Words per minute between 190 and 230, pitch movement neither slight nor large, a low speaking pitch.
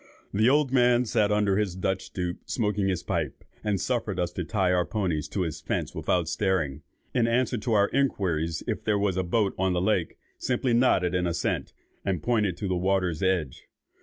Yes: average, 200 wpm; average, 3.6 semitones; very low, 95 Hz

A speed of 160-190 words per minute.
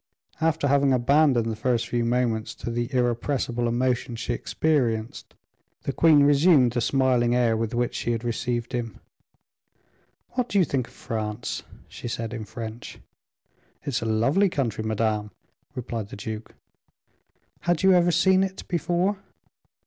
No: average, 150 wpm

